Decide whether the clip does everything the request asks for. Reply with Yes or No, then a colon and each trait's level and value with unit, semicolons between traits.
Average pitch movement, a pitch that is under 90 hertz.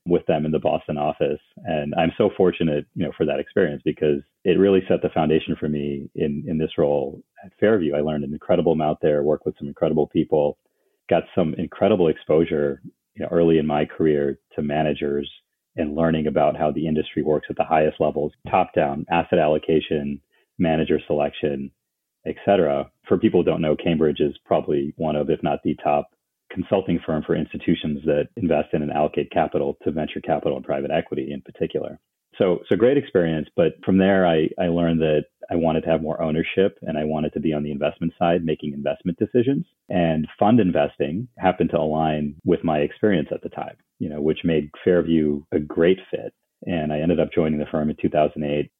No: narrow, 1.9 semitones; very low, 75 Hz